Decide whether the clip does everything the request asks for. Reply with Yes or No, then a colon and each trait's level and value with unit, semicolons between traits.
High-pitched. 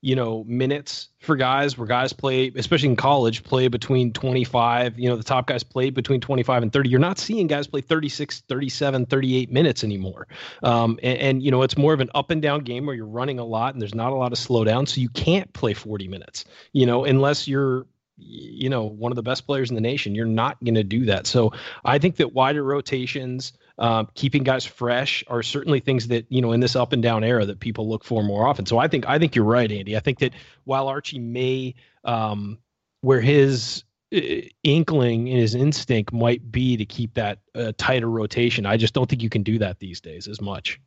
No: low, 125 Hz